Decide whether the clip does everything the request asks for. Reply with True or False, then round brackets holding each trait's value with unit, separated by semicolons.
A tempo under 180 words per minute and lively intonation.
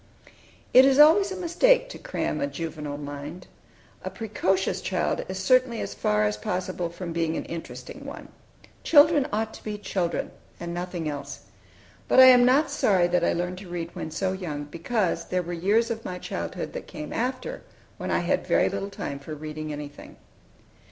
False (185 wpm; 7.3 semitones)